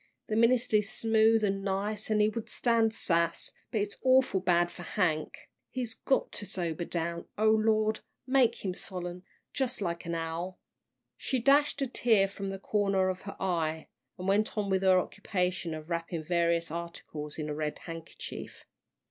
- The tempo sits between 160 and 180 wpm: Yes, average, 175 wpm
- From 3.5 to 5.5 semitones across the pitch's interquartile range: Yes, average, 4.3 semitones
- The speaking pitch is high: Yes, high, 195 Hz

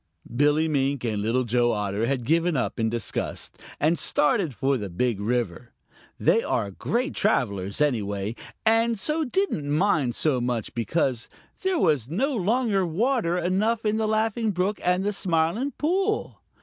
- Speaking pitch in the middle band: Yes, medium, 160 Hz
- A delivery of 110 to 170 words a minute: Yes, average, 155 wpm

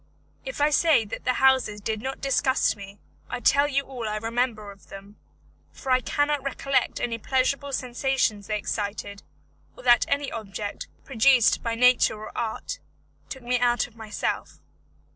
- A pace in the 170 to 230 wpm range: No, average, 160 wpm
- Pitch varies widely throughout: No, average, 3.8 semitones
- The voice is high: Yes, high, 245 Hz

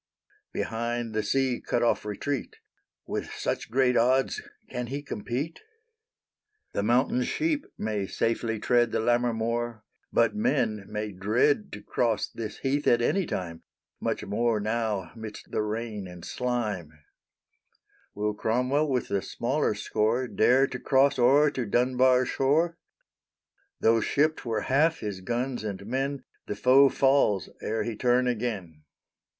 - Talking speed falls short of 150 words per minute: Yes, average, 140 wpm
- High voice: No, low, 120 Hz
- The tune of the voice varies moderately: Yes, average, 3.6 semitones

